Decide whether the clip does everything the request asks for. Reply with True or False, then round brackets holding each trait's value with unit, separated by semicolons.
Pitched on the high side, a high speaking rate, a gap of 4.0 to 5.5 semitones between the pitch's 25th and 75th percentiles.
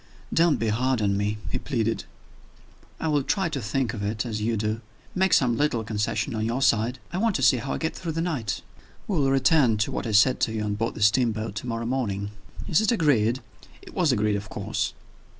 False (115 Hz; 225 wpm; 5.0 semitones)